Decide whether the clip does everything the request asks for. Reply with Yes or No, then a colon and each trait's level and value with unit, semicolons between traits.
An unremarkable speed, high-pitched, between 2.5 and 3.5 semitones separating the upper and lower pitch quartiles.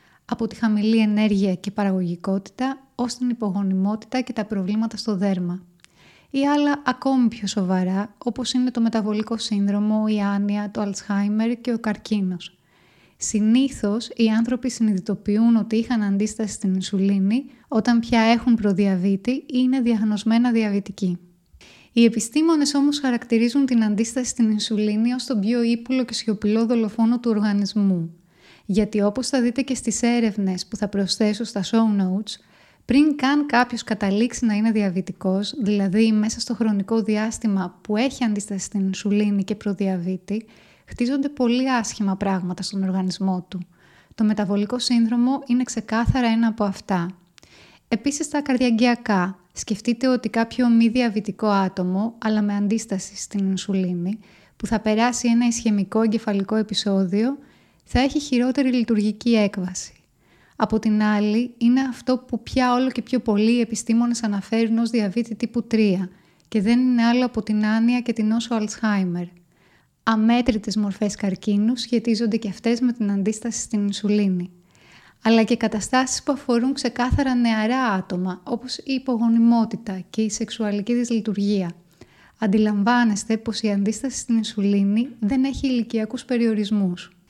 Yes: average, 140 wpm; high, 220 Hz; average, 3.0 semitones